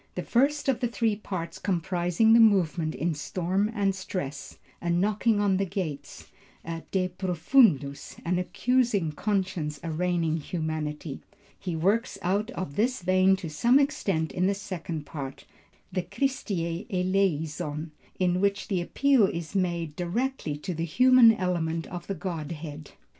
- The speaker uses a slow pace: No, average, 145 wpm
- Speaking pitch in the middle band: Yes, medium, 180 Hz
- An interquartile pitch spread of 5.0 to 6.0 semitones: No, average, 4.0 semitones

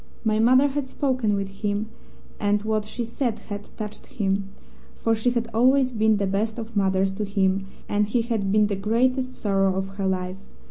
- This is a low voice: No, high, 215 Hz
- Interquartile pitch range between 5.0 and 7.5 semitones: No, average, 2.9 semitones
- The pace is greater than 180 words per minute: Yes, average, 190 wpm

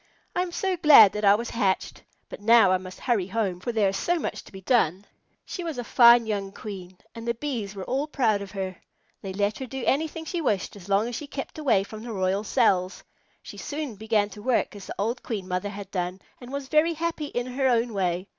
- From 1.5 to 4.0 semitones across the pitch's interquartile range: No, average, 5.2 semitones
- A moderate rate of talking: No, fast, 240 wpm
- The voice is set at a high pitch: Yes, high, 220 Hz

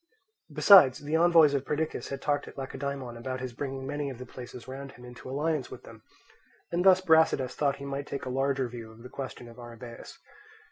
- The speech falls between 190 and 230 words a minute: Yes, fast, 205 wpm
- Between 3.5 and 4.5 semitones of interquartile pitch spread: No, narrow, 2.5 semitones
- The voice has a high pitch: No, low, 135 Hz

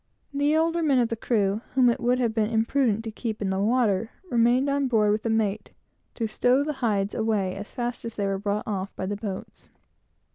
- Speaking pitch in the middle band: No, high, 225 Hz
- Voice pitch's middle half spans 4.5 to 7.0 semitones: No, average, 3.3 semitones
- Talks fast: Yes, fast, 225 wpm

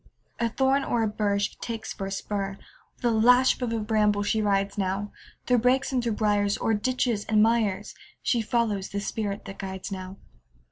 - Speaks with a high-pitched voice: Yes, high, 210 Hz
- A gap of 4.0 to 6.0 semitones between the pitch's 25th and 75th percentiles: No, narrow, 2.6 semitones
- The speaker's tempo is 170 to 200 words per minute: Yes, average, 195 wpm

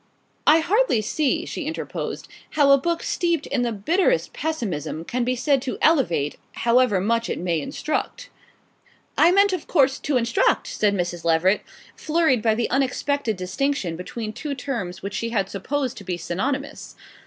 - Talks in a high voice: Yes, very high, 250 Hz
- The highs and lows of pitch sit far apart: Yes, wide, 7.1 semitones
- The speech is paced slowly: No, average, 165 wpm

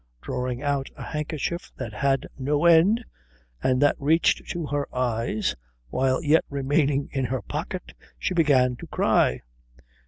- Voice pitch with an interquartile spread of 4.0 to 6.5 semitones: No, average, 3.4 semitones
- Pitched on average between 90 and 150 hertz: Yes, medium, 140 Hz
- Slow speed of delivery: No, average, 145 wpm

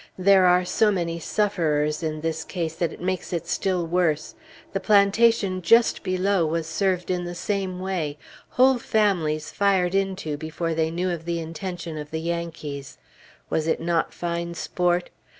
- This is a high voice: No, medium, 175 Hz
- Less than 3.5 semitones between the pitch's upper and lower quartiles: Yes, average, 2.8 semitones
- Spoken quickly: No, average, 165 wpm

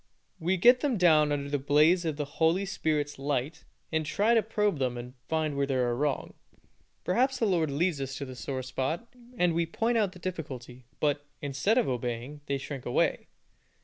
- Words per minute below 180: No, average, 195 wpm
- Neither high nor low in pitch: Yes, medium, 150 Hz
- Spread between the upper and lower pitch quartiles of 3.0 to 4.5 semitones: No, average, 4.9 semitones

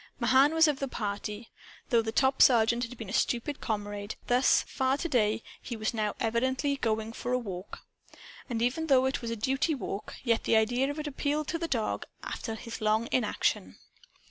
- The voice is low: No, high, 240 Hz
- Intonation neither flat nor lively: Yes, average, 3.4 semitones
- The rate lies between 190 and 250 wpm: Yes, average, 195 wpm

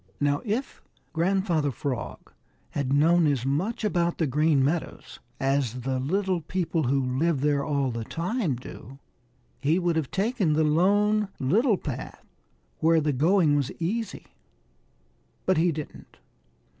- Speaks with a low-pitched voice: No, medium, 155 Hz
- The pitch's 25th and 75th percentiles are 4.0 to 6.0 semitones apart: Yes, average, 4.9 semitones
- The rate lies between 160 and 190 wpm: No, average, 140 wpm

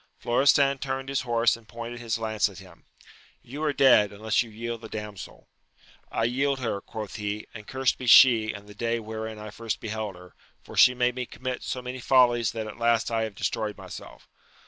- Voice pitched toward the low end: Yes, low, 115 Hz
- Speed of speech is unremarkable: No, fast, 210 wpm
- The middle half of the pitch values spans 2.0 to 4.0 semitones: Yes, average, 2.7 semitones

